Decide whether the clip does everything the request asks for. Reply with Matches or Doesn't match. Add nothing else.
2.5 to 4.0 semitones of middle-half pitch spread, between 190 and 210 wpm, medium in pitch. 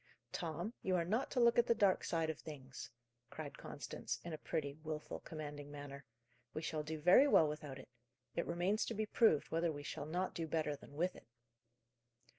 Matches